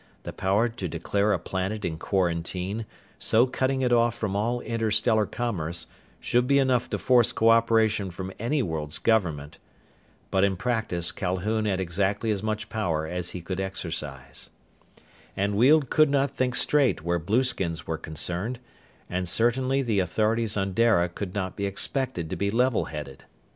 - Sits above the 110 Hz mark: No, low, 105 Hz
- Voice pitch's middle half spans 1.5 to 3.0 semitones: No, average, 4.7 semitones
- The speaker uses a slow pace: No, average, 160 wpm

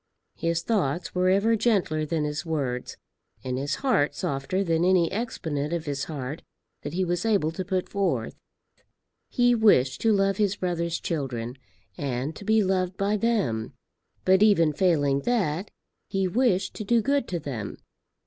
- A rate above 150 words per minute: Yes, average, 160 wpm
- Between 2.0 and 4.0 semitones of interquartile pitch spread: No, wide, 5.5 semitones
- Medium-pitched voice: Yes, medium, 175 Hz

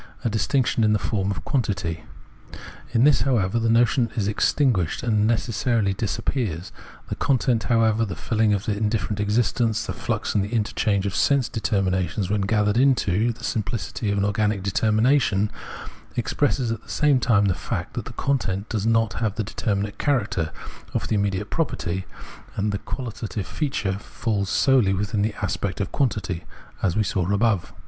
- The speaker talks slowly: No, average, 170 wpm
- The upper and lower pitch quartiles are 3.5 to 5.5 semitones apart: No, average, 2.8 semitones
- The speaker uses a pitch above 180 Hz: No, low, 105 Hz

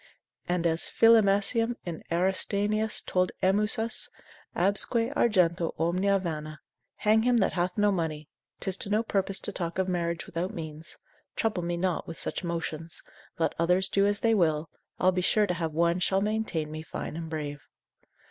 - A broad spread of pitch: No, average, 3.5 semitones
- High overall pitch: No, medium, 180 Hz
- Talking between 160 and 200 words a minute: Yes, average, 165 wpm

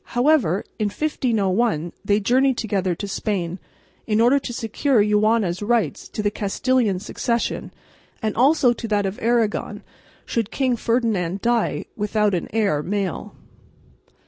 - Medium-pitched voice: No, high, 215 Hz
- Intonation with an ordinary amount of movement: Yes, average, 3.3 semitones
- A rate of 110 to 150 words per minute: Yes, slow, 135 wpm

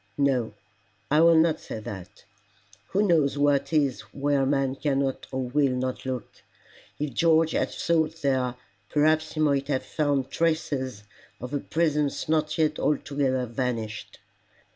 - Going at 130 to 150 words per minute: Yes, average, 140 wpm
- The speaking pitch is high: No, medium, 140 Hz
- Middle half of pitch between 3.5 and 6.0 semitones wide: No, average, 3.0 semitones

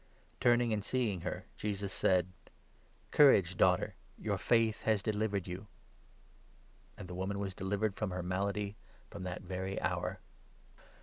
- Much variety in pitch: No, narrow, 2.6 semitones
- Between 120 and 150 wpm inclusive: Yes, average, 145 wpm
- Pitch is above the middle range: No, low, 100 Hz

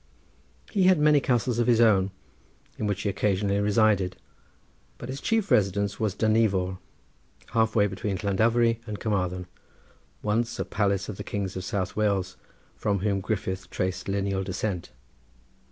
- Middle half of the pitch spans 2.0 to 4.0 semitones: Yes, narrow, 2.6 semitones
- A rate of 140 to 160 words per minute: Yes, average, 150 wpm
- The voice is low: Yes, low, 100 Hz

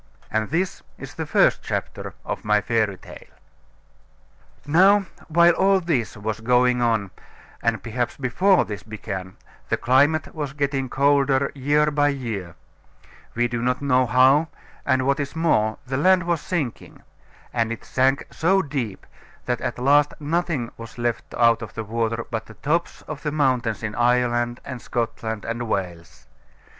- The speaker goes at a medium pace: Yes, average, 155 wpm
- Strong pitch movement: No, average, 4.2 semitones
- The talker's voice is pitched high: No, low, 125 Hz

